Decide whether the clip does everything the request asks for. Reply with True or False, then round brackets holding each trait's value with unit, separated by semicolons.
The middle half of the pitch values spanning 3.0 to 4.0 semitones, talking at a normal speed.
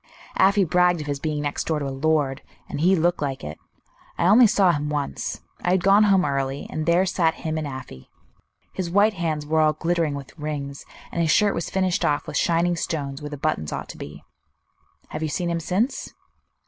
False (3.5 semitones; 210 wpm)